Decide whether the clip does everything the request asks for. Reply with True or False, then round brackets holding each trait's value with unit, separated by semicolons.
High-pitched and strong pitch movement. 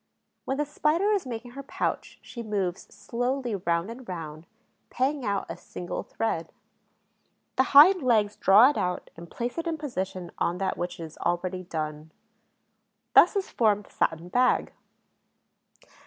True (215 Hz; 7.0 semitones)